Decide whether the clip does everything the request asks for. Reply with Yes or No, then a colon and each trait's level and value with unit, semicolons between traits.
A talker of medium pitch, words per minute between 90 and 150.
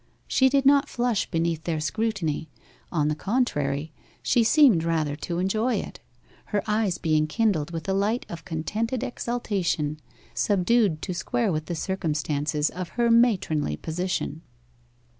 Yes: medium, 180 Hz; average, 140 wpm